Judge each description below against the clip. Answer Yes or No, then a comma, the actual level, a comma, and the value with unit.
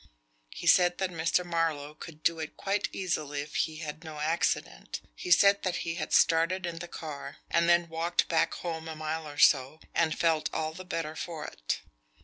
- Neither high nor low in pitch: Yes, medium, 165 Hz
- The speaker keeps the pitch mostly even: Yes, narrow, 1.8 semitones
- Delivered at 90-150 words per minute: No, average, 195 wpm